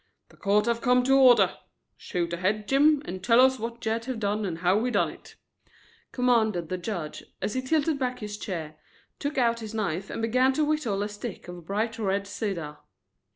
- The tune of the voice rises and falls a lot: No, average, 4.3 semitones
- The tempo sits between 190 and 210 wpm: Yes, average, 200 wpm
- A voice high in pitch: Yes, high, 220 Hz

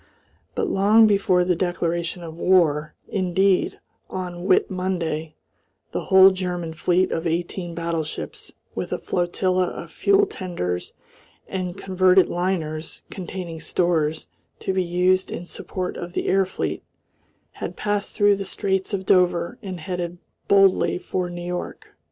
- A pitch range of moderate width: No, narrow, 1.7 semitones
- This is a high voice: No, medium, 180 Hz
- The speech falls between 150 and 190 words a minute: No, average, 140 wpm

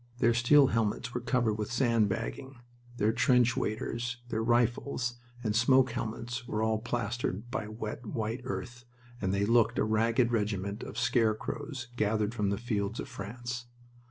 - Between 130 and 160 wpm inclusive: Yes, average, 155 wpm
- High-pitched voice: No, low, 115 Hz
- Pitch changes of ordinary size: No, narrow, 2.1 semitones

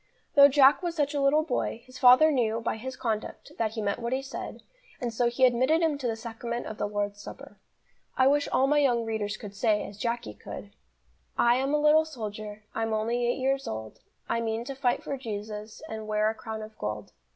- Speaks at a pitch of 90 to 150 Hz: No, high, 235 Hz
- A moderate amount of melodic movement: Yes, average, 3.7 semitones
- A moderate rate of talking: No, fast, 220 wpm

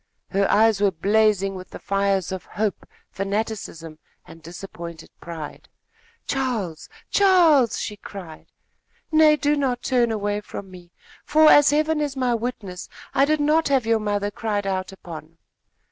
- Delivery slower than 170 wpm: Yes, average, 145 wpm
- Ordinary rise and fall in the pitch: No, wide, 6.0 semitones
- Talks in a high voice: Yes, high, 205 Hz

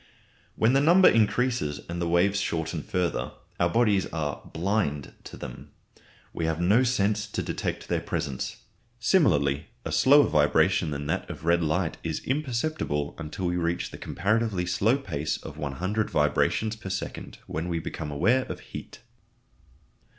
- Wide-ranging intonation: Yes, wide, 6.1 semitones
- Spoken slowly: No, average, 155 wpm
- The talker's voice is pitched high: No, very low, 90 Hz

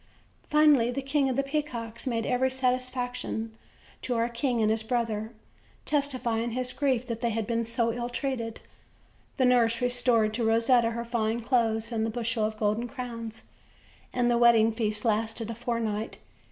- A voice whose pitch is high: Yes, high, 235 Hz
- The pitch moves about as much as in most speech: No, narrow, 1.8 semitones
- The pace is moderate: Yes, average, 175 wpm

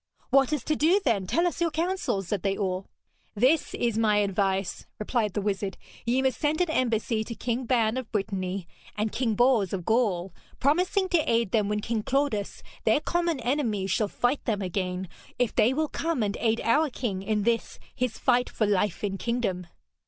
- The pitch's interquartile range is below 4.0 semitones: No, average, 4.7 semitones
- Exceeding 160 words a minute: Yes, average, 190 wpm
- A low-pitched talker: No, high, 225 Hz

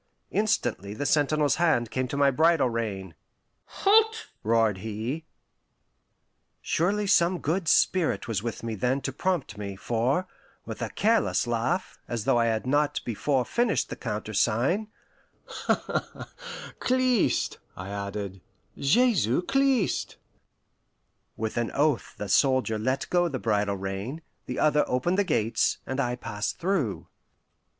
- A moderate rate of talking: No, slow, 130 wpm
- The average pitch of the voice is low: Yes, low, 130 Hz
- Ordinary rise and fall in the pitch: No, wide, 7.9 semitones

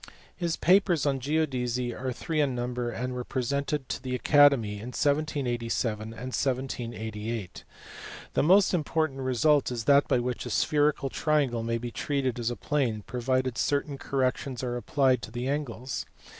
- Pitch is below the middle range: Yes, low, 130 Hz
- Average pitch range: Yes, average, 3.1 semitones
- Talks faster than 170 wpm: No, average, 155 wpm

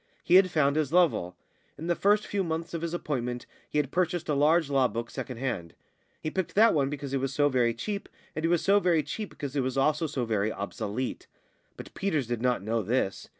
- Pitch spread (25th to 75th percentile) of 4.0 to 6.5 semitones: Yes, wide, 5.4 semitones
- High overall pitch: No, medium, 145 Hz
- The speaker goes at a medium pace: No, fast, 230 wpm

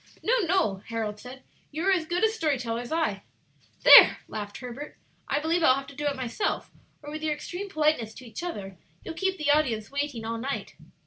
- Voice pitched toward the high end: Yes, very high, 290 Hz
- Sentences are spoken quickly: Yes, fast, 210 wpm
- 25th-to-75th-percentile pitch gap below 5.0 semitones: No, wide, 5.6 semitones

